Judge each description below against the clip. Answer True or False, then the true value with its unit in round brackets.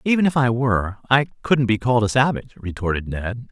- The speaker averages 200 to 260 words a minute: True (205 wpm)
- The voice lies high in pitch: False (120 Hz)